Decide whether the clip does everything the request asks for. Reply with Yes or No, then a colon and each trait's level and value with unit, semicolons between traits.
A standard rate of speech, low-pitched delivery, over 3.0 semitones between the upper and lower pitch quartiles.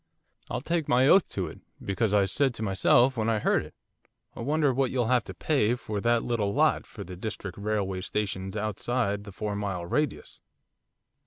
Yes: average, 190 wpm; low, 110 Hz; average, 3.9 semitones